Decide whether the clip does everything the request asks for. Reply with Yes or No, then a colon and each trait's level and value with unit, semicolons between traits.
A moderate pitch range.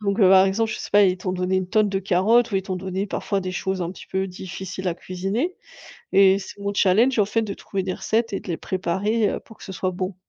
No: narrow, 1.9 semitones